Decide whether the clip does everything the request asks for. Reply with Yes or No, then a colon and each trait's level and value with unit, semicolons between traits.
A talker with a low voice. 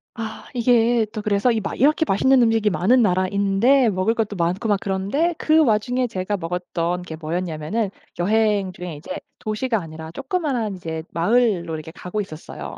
No: high, 205 Hz